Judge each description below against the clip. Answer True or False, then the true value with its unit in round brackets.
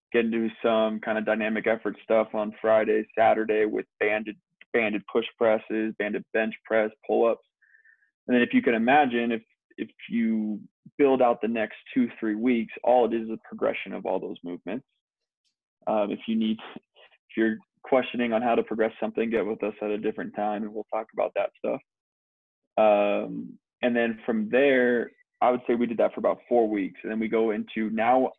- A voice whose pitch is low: True (110 Hz)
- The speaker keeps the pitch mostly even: True (1.8 semitones)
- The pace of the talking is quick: False (195 wpm)